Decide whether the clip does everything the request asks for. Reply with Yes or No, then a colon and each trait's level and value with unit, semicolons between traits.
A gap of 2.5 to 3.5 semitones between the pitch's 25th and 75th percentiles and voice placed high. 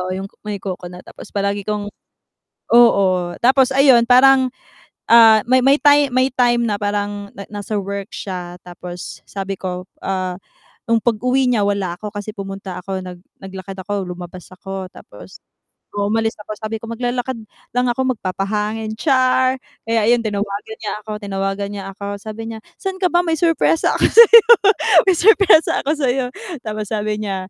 No: average, 4.2 semitones; high, 215 Hz